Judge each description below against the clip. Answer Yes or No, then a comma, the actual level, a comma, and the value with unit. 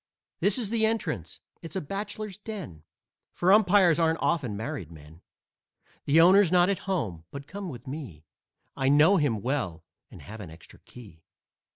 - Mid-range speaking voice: Yes, medium, 155 Hz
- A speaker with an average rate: Yes, average, 165 wpm